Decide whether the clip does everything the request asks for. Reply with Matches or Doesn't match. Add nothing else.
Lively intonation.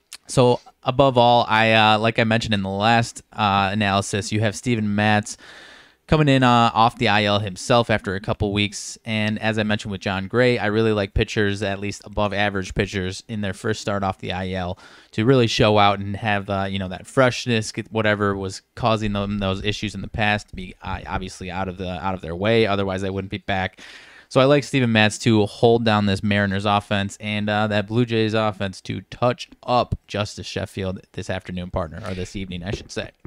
Doesn't match